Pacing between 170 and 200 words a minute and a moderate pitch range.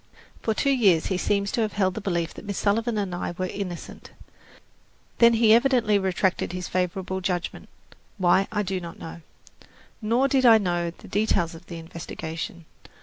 Yes: average, 175 wpm; average, 3.7 semitones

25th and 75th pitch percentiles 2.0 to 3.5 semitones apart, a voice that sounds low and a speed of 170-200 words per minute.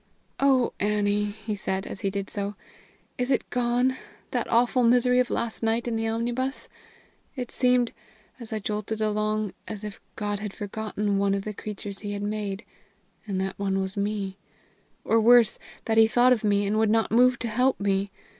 No: average, 2.7 semitones; high, 215 Hz; average, 185 wpm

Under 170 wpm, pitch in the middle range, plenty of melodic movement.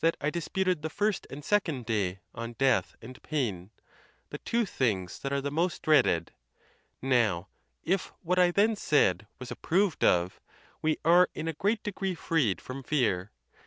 Yes: average, 160 wpm; medium, 145 Hz; wide, 7.8 semitones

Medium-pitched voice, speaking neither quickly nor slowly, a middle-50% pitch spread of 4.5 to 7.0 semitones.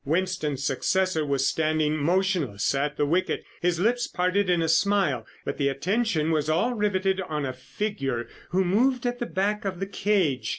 Yes: medium, 175 Hz; average, 180 wpm; average, 5.1 semitones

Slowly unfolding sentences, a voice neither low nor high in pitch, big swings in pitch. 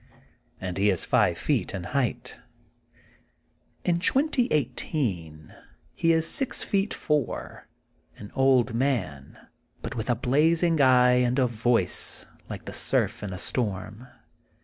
No: slow, 125 wpm; low, 125 Hz; wide, 6.6 semitones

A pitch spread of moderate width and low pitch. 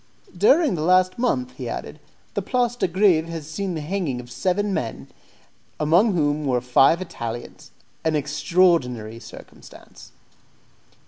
No: average, 5.0 semitones; medium, 165 Hz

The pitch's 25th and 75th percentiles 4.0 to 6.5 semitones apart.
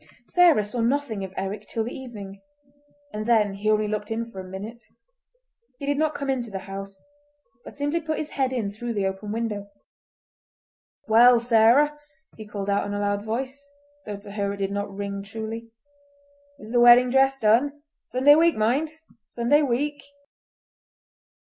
Yes: average, 4.7 semitones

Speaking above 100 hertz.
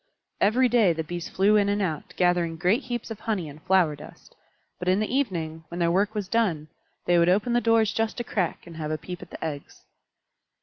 Yes: medium, 185 Hz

